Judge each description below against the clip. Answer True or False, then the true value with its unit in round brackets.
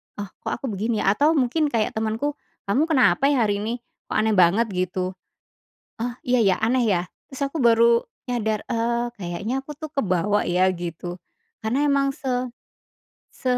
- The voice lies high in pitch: True (230 Hz)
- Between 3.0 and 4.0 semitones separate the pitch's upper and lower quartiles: False (4.7 semitones)